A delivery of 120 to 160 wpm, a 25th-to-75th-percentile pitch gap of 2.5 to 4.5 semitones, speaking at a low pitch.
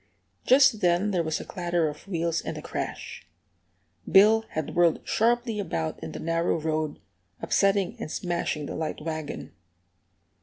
No: average, 150 wpm; average, 4.2 semitones; medium, 170 Hz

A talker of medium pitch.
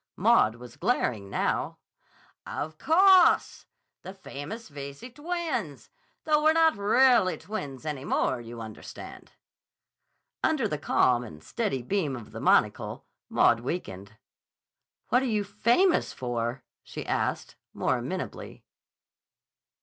Yes: medium, 170 Hz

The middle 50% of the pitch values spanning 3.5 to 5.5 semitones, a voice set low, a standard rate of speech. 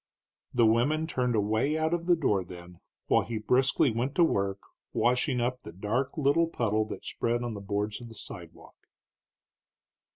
Yes: average, 4.7 semitones; low, 120 Hz; average, 170 wpm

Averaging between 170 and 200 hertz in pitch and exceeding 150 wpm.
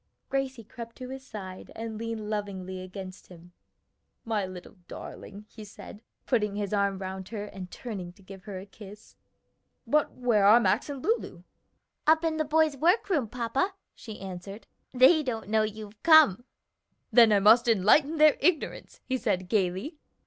No: high, 215 Hz; average, 165 wpm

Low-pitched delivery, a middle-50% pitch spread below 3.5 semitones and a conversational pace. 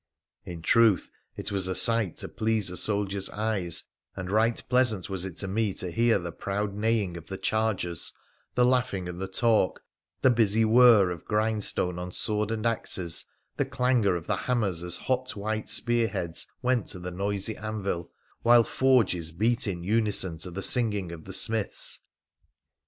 No: low, 105 Hz; average, 3.8 semitones; average, 175 wpm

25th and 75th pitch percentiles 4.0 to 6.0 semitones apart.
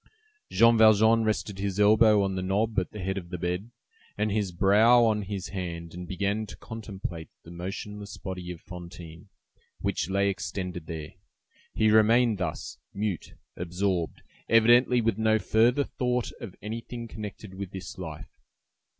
No: average, 3.3 semitones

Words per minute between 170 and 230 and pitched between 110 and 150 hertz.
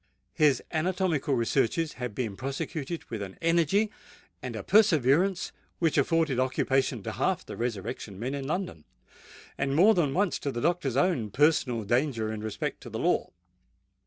No: average, 160 wpm; medium, 140 Hz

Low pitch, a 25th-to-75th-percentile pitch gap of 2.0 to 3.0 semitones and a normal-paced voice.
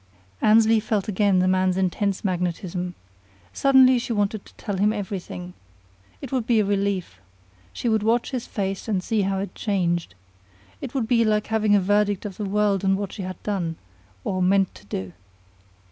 No: high, 200 Hz; narrow, 2.6 semitones; average, 180 wpm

